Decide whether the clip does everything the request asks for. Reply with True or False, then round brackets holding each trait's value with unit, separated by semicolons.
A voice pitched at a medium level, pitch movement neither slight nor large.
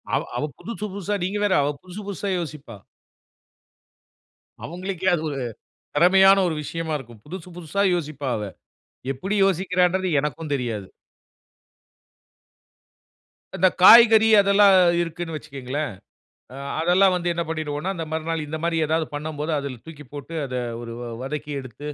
True (165 Hz; 4.3 semitones)